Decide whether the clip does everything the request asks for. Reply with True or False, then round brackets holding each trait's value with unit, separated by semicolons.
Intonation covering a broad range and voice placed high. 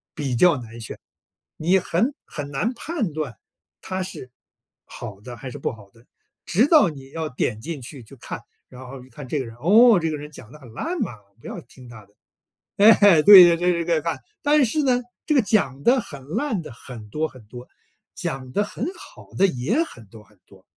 False (7.8 semitones; 150 Hz)